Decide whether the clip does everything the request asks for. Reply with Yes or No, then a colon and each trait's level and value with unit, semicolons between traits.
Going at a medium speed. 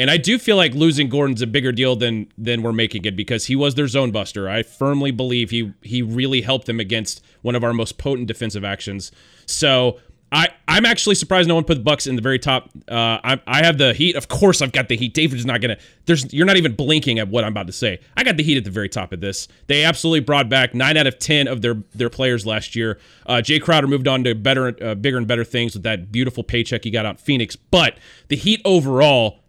No: fast, 255 wpm